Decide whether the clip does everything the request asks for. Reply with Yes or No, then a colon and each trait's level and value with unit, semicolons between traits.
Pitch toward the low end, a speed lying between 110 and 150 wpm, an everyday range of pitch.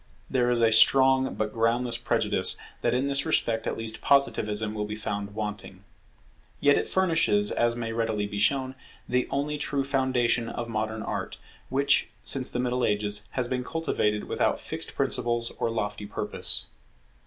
No: low, 120 Hz; average, 165 wpm; average, 3.5 semitones